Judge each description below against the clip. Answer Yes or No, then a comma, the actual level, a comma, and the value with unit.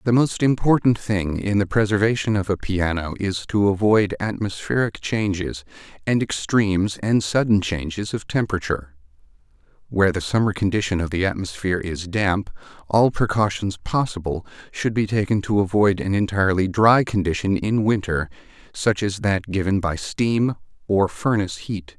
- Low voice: Yes, low, 100 Hz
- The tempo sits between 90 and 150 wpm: Yes, average, 145 wpm